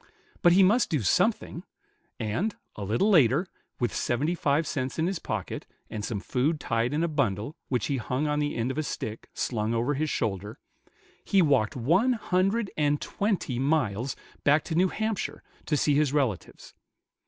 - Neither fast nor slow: Yes, average, 175 wpm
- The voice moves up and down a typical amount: No, wide, 6.2 semitones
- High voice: No, medium, 145 Hz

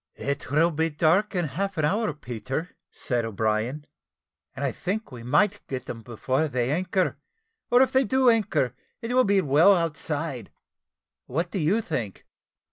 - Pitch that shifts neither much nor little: No, wide, 7.1 semitones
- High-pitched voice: No, medium, 155 Hz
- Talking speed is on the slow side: No, average, 165 wpm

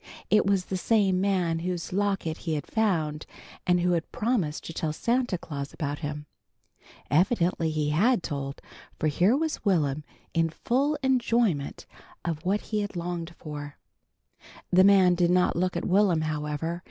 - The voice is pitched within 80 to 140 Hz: No, medium, 175 Hz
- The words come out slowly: No, average, 160 wpm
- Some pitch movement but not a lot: Yes, average, 4.3 semitones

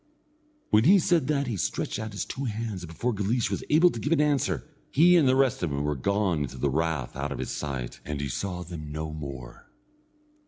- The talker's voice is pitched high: No, low, 100 Hz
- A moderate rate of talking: No, fast, 230 wpm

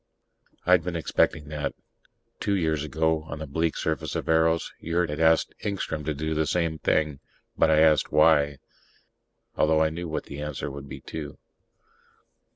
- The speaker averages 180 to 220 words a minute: No, average, 165 wpm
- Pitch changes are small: Yes, narrow, 1.4 semitones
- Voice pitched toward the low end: Yes, very low, 80 Hz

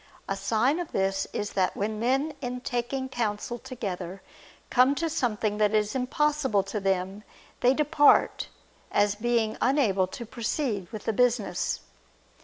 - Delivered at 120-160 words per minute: Yes, average, 145 wpm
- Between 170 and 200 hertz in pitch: No, high, 225 Hz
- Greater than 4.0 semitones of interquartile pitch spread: Yes, average, 4.4 semitones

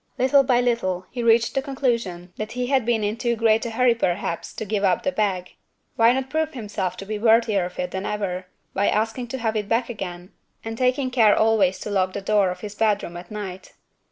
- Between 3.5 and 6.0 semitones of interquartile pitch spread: Yes, average, 3.9 semitones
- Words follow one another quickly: Yes, fast, 225 wpm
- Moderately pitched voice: No, high, 220 Hz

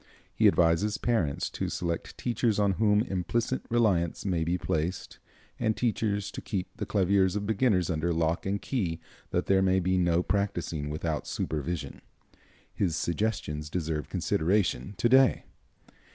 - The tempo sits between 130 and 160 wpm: Yes, average, 145 wpm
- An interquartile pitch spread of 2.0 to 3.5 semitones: No, average, 3.9 semitones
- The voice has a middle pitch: No, very low, 95 Hz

